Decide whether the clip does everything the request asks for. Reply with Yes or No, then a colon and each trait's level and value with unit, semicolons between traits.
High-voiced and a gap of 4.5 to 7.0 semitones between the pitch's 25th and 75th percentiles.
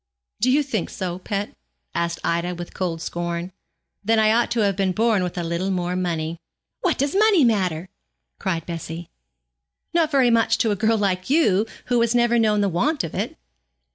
Yes: high, 195 Hz; average, 5.2 semitones